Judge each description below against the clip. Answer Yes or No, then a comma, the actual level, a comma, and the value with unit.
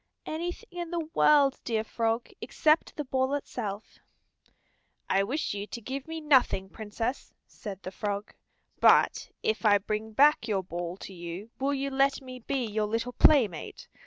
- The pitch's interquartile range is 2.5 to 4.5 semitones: No, average, 5.2 semitones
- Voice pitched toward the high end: Yes, high, 230 Hz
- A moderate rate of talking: Yes, average, 160 wpm